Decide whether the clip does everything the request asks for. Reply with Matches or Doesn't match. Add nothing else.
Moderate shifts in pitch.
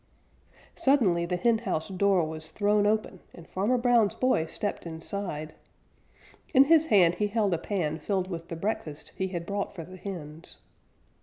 Matches